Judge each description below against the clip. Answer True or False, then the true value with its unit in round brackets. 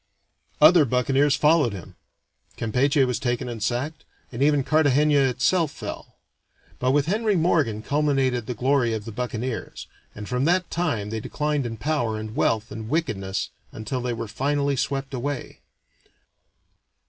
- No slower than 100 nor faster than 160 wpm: True (150 wpm)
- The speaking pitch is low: True (130 Hz)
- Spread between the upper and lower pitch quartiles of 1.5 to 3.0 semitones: False (4.3 semitones)